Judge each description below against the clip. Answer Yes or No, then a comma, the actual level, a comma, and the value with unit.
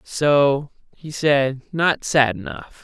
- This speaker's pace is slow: Yes, slow, 125 wpm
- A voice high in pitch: No, medium, 140 Hz